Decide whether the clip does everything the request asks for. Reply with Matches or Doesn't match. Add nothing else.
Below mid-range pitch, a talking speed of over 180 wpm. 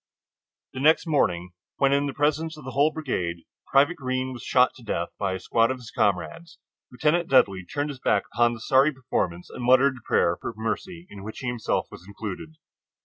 Matches